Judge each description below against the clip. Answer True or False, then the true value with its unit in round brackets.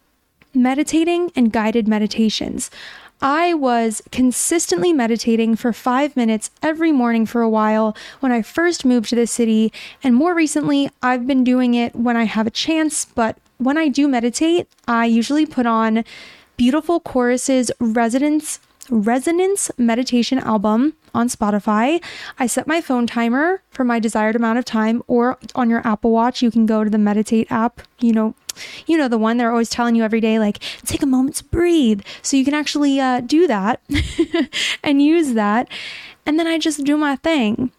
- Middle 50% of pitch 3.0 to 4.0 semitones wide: False (4.5 semitones)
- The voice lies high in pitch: True (250 Hz)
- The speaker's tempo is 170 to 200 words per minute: True (175 wpm)